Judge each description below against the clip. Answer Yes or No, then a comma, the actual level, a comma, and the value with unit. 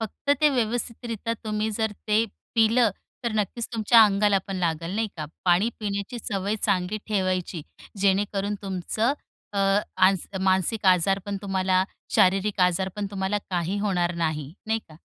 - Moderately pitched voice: No, high, 200 Hz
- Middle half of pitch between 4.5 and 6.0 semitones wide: No, average, 2.8 semitones